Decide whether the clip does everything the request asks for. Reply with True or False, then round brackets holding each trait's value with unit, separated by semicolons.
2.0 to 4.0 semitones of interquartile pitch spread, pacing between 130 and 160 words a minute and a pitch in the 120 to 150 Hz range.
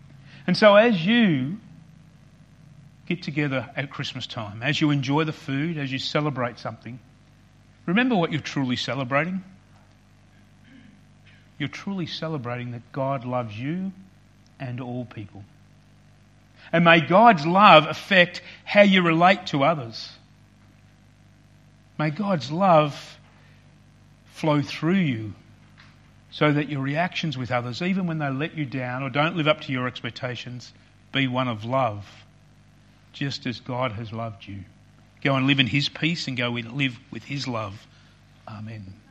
False (4.7 semitones; 140 wpm; 135 Hz)